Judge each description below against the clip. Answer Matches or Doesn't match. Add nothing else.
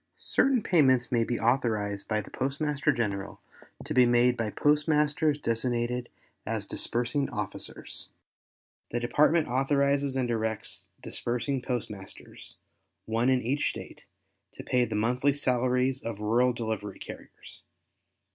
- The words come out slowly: Matches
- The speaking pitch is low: Matches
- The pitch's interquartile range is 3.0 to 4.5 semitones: Matches